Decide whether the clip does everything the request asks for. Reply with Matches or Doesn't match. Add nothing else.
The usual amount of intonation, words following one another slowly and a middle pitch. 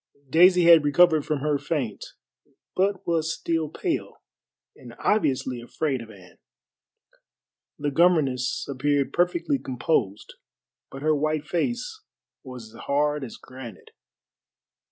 Matches